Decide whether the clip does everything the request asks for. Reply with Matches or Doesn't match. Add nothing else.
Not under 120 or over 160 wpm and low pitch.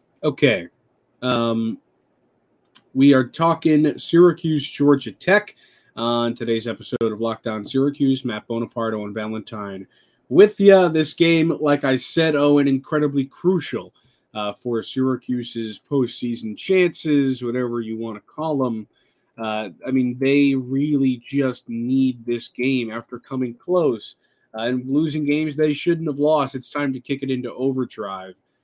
Matches